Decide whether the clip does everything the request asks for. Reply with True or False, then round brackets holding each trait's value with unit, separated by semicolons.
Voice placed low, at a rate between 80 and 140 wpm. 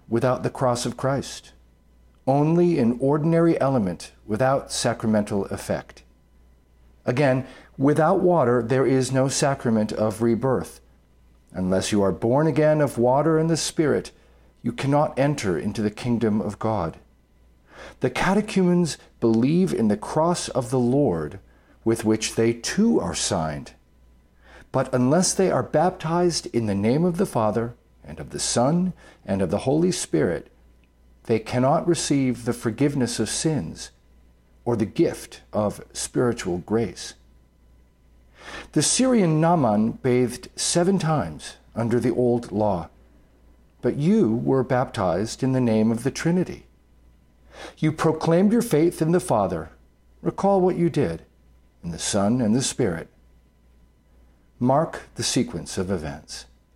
True (115 Hz; 135 wpm)